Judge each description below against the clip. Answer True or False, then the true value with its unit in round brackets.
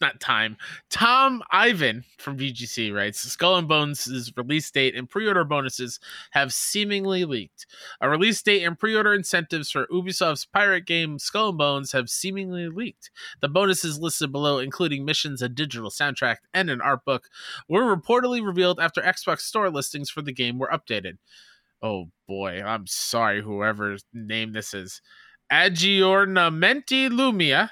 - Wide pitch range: True (7.3 semitones)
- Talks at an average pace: True (155 wpm)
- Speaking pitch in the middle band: True (155 Hz)